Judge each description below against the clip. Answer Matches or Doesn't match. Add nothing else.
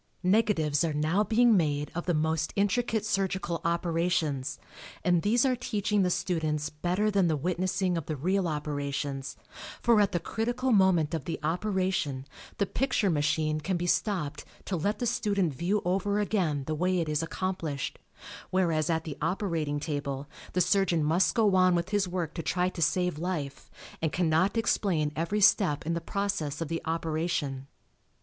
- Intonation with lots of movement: Doesn't match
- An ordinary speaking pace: Matches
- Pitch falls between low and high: Matches